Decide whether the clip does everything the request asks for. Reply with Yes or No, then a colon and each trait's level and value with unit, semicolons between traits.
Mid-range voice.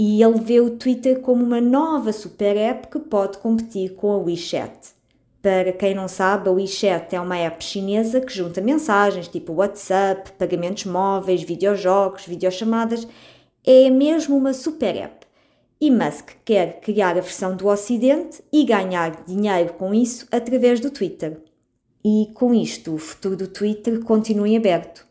No: high, 205 Hz